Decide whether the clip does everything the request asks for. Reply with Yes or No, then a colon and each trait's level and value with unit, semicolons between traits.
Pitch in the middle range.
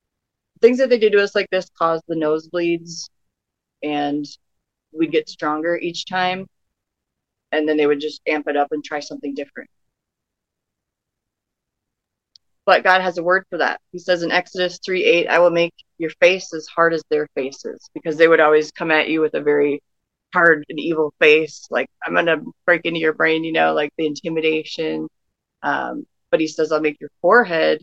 Yes: medium, 160 Hz